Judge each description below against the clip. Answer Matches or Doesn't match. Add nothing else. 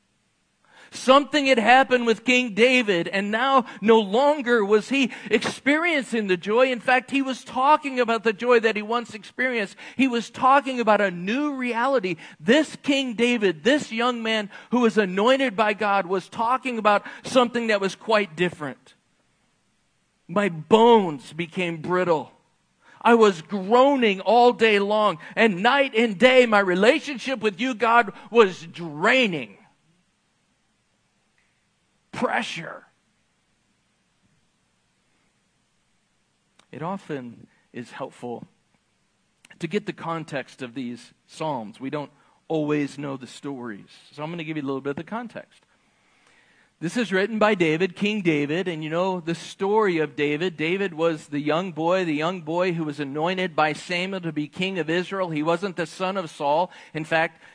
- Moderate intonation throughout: Doesn't match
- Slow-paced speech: Doesn't match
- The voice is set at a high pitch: Matches